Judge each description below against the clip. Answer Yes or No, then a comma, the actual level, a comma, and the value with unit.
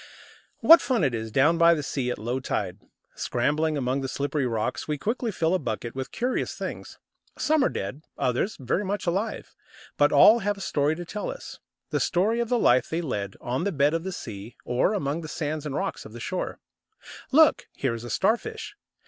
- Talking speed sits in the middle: No, fast, 210 wpm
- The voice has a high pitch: No, medium, 150 Hz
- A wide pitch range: Yes, wide, 7.8 semitones